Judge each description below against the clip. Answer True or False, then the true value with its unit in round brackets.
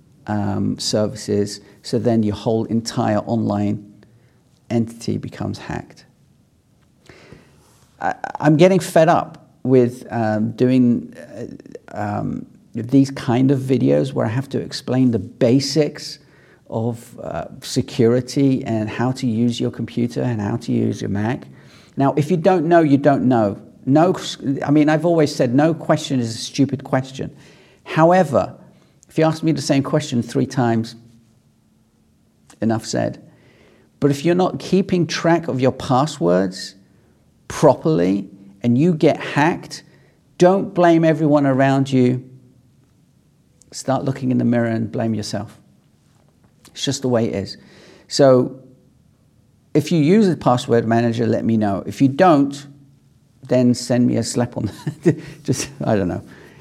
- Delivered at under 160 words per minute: True (145 wpm)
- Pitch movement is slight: False (4.1 semitones)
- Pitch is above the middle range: False (130 Hz)